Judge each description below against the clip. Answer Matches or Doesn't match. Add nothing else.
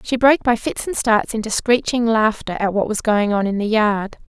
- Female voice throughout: Matches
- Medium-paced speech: Doesn't match